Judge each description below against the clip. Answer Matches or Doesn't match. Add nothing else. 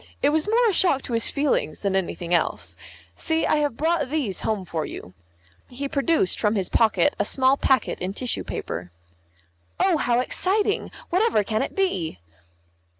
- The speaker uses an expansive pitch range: Matches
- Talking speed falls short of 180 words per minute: Matches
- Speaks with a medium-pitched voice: Doesn't match